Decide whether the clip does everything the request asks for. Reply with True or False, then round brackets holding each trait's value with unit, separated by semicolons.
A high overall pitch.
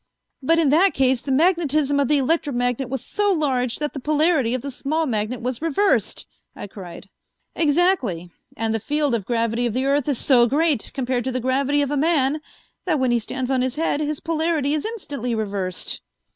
True (270 Hz)